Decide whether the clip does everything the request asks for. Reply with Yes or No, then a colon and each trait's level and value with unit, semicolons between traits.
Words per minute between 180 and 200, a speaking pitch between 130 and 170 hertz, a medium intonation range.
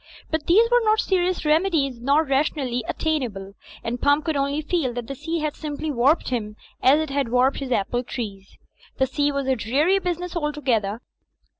No: average, 185 wpm; very high, 280 Hz; average, 4.3 semitones